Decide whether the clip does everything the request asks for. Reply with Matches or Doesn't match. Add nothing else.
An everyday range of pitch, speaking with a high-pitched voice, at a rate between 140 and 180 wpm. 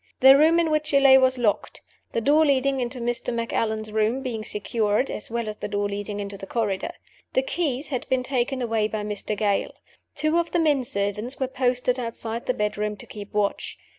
Doesn't match